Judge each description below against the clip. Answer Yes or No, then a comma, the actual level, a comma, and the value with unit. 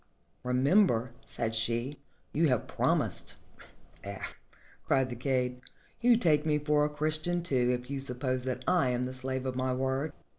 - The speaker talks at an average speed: Yes, average, 175 wpm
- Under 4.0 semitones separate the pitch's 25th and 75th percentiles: Yes, average, 3.0 semitones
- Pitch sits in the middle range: No, low, 130 Hz